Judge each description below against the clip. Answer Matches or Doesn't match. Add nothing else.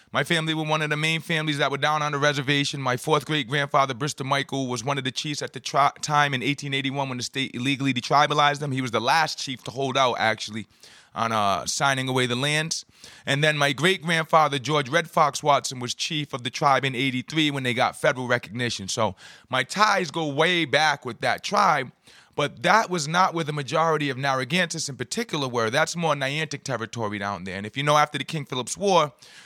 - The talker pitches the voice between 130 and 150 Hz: Matches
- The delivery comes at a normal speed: Doesn't match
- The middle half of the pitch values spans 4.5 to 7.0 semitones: Doesn't match